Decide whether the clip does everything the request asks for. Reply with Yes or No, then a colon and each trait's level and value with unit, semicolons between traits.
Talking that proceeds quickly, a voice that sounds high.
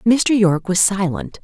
No: average, 165 wpm; high, 200 Hz